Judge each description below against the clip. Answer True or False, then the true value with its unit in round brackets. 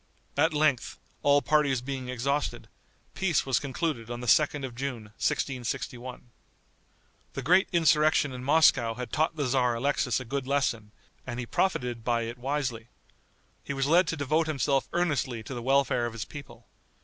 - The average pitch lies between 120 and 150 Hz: True (135 Hz)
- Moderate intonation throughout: True (3.5 semitones)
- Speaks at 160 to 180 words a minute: True (165 wpm)